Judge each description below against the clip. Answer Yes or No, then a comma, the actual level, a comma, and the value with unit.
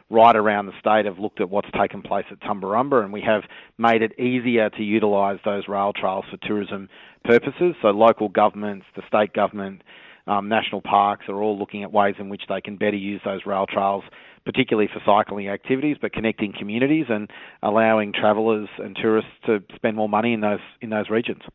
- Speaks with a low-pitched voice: Yes, low, 105 Hz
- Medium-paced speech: Yes, average, 195 wpm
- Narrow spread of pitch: Yes, narrow, 1.8 semitones